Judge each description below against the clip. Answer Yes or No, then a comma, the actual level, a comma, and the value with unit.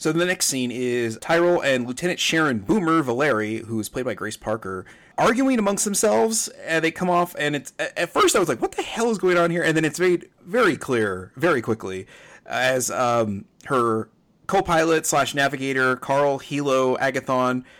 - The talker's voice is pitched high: No, medium, 140 Hz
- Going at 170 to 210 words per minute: Yes, average, 185 wpm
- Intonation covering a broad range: Yes, wide, 5.9 semitones